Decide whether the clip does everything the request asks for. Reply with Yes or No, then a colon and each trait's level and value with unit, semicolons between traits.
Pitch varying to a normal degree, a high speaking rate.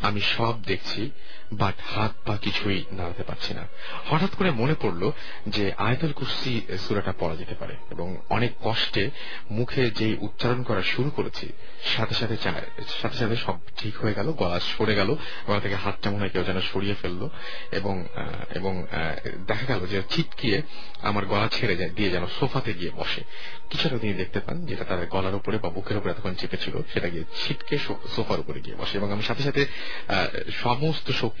Yes: average, 4.0 semitones; fast, 155 wpm